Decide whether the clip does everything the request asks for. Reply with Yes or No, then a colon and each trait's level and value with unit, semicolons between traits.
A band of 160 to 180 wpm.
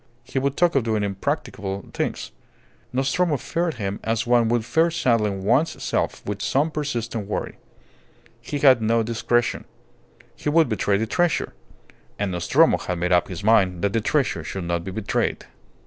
Yes: average, 165 wpm